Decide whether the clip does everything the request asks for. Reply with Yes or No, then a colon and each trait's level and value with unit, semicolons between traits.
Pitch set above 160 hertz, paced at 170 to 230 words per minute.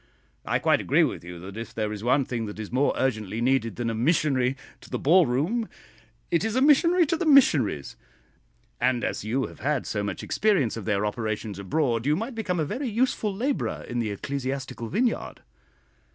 No: low, 130 Hz; average, 195 wpm